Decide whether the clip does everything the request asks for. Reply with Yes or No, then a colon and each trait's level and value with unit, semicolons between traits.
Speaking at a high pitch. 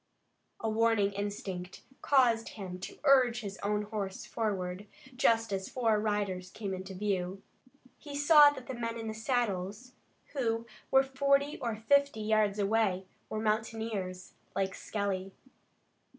Yes: high, 215 Hz